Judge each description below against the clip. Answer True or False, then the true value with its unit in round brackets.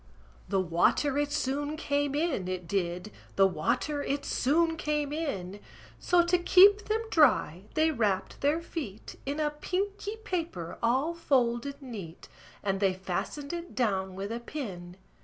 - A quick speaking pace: False (150 wpm)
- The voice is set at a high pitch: True (275 Hz)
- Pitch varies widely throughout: True (8.5 semitones)